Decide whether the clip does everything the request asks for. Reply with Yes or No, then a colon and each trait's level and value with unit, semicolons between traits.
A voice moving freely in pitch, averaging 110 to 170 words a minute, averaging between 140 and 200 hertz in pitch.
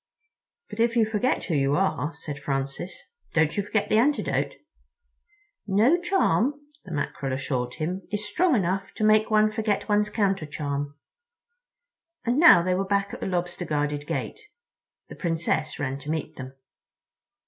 Yes: wide, 6.6 semitones; average, 160 wpm; high, 190 Hz